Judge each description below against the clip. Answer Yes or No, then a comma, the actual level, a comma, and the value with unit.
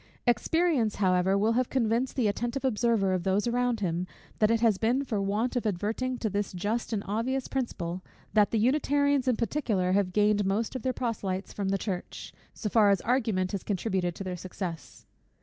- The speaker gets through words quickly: No, average, 190 wpm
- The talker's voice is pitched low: No, high, 215 Hz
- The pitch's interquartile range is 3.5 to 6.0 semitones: Yes, average, 4.0 semitones